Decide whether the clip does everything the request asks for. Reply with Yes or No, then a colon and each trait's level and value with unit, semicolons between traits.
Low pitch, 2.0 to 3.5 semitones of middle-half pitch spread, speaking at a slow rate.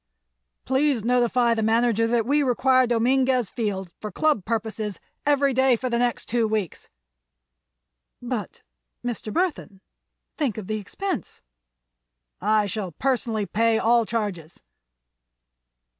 No: high, 230 Hz; average, 3.1 semitones; slow, 115 wpm